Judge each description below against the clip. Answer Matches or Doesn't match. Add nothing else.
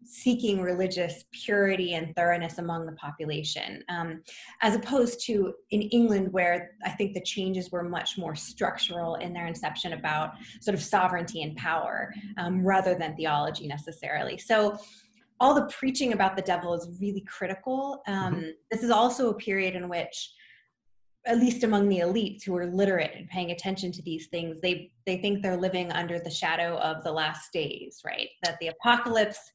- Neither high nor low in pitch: Matches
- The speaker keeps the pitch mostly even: Doesn't match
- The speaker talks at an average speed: Matches